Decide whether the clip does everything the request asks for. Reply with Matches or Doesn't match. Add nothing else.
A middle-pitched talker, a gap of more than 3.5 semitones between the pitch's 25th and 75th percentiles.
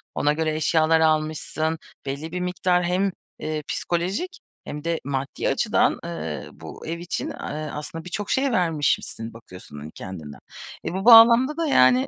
Matches